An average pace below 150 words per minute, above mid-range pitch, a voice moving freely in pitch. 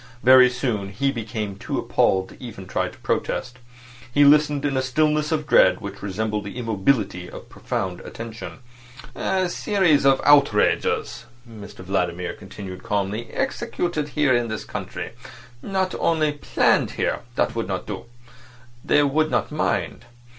No: average, 140 wpm; low, 120 Hz; wide, 6.0 semitones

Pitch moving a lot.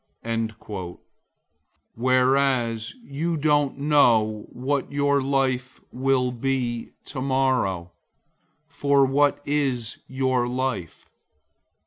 No: average, 2.9 semitones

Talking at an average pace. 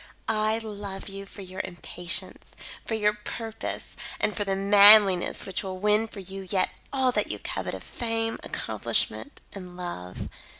Yes: average, 160 wpm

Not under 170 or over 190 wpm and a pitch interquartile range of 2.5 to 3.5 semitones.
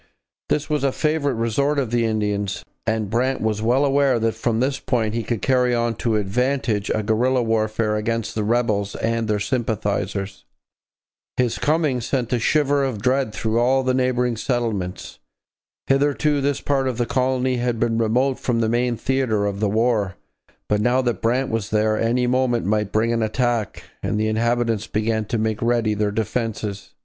Yes: average, 180 wpm; average, 2.9 semitones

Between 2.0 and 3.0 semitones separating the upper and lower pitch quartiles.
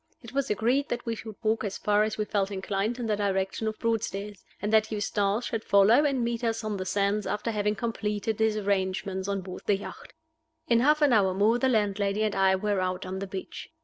Yes: narrow, 2.4 semitones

